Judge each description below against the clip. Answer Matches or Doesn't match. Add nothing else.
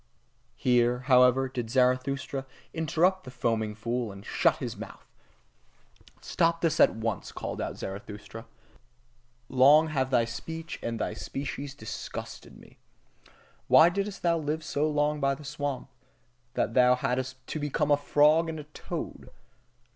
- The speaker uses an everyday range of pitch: Matches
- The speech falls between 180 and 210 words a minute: Doesn't match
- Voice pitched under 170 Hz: Matches